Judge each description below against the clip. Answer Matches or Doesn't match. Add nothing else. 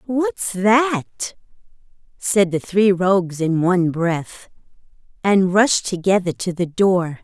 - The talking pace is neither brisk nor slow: Doesn't match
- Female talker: Matches